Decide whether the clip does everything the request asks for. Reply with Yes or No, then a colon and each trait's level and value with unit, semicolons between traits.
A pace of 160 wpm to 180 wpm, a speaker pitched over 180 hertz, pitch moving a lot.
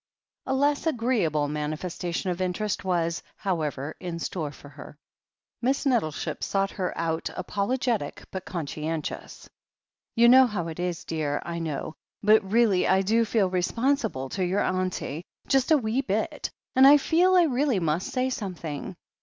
Yes: average, 165 wpm; high, 190 Hz; wide, 6.5 semitones